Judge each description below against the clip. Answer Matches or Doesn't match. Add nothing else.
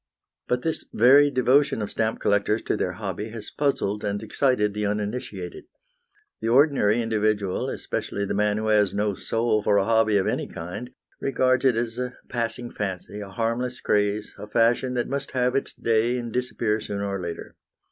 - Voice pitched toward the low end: Matches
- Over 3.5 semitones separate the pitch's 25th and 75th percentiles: Doesn't match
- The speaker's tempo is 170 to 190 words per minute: Matches